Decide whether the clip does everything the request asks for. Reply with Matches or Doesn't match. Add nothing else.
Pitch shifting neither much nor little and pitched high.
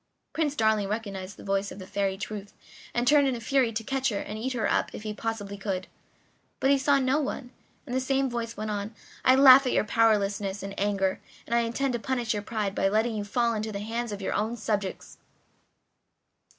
Matches